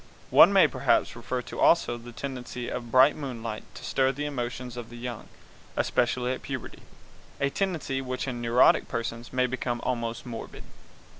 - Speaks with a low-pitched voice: Yes, low, 125 Hz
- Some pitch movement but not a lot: No, narrow, 1.8 semitones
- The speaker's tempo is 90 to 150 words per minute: No, average, 165 wpm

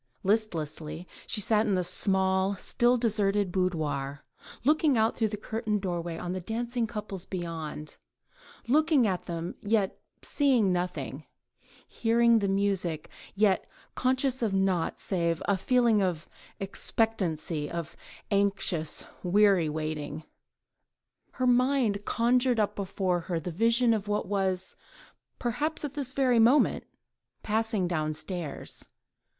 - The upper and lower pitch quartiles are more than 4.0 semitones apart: Yes, average, 4.7 semitones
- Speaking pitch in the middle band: No, high, 200 Hz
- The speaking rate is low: Yes, slow, 120 wpm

